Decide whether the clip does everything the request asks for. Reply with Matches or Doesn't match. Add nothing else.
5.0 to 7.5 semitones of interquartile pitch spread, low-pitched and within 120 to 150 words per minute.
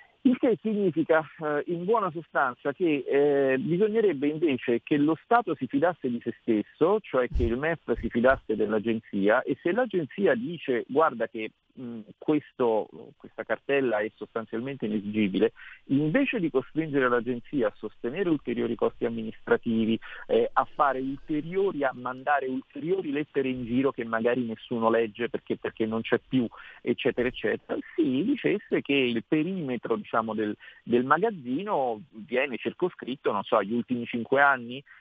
Matches